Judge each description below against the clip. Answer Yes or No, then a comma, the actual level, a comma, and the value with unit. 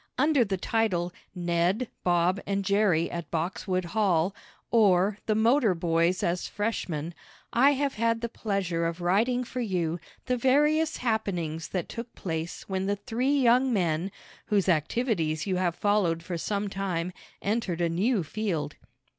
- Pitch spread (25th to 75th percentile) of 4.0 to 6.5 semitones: Yes, average, 4.9 semitones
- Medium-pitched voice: No, high, 195 Hz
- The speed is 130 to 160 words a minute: Yes, average, 150 wpm